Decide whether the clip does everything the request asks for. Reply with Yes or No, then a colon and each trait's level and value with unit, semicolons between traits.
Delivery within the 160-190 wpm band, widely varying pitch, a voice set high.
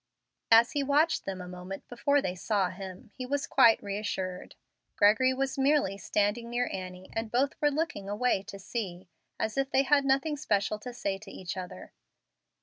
Yes: average, 180 wpm; wide, 5.8 semitones; high, 220 Hz